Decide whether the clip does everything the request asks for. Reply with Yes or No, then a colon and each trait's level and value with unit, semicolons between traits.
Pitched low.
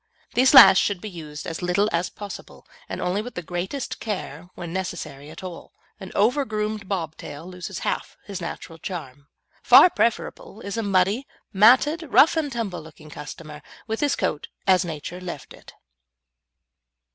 No: medium, 185 Hz